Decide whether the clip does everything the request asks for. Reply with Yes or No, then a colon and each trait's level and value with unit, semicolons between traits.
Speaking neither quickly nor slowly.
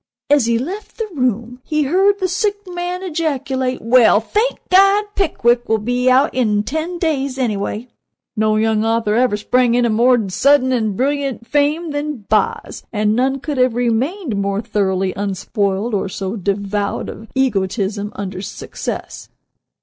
Yes: average, 150 wpm